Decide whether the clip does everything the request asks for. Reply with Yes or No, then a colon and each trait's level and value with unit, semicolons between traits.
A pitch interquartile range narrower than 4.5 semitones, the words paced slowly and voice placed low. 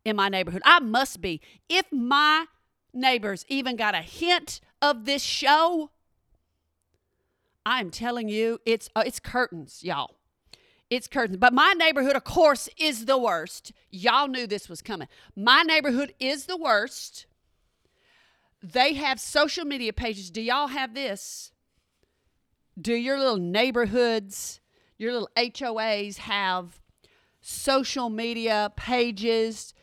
No: average, 4.1 semitones; slow, 130 wpm; high, 245 Hz